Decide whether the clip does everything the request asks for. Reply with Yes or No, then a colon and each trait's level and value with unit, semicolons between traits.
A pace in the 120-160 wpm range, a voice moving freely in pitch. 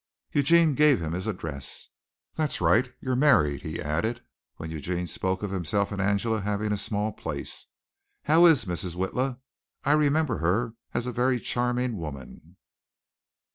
Yes: average, 150 wpm; wide, 6.3 semitones